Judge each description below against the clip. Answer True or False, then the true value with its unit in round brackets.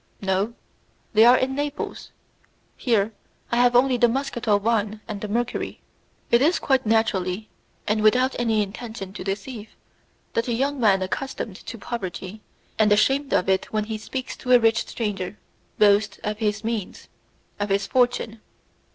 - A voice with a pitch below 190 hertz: False (220 Hz)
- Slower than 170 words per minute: True (160 wpm)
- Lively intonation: False (3.0 semitones)